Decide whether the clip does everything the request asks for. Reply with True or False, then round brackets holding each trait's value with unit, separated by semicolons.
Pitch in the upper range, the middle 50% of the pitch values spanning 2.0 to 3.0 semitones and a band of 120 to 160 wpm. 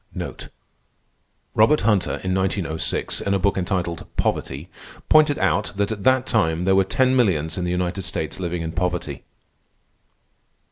False (95 Hz; 2.7 semitones; 145 wpm)